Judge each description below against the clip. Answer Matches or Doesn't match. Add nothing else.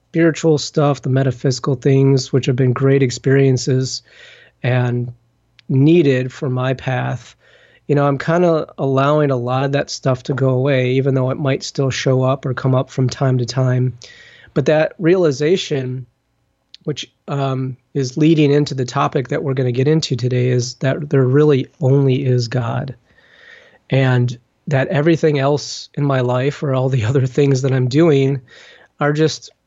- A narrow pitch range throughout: Matches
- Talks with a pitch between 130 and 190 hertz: Matches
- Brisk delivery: Doesn't match